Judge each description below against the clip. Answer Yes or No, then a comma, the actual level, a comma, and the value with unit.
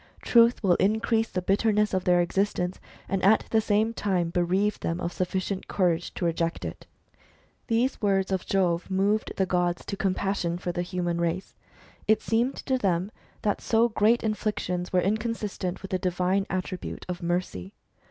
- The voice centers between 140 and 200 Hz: Yes, high, 190 Hz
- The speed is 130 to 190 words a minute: Yes, average, 170 wpm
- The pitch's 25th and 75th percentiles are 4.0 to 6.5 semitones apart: No, average, 3.0 semitones